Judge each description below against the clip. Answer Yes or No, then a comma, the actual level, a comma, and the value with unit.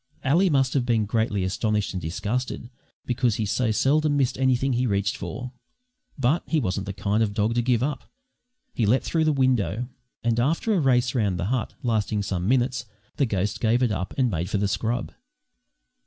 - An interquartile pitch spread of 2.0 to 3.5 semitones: No, average, 4.0 semitones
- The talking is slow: No, average, 195 wpm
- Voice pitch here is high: No, low, 120 Hz